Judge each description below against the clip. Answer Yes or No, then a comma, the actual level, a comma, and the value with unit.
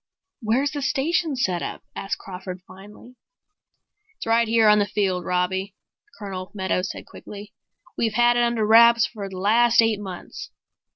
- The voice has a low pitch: No, high, 210 Hz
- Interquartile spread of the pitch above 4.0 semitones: No, average, 3.7 semitones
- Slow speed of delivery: No, average, 160 wpm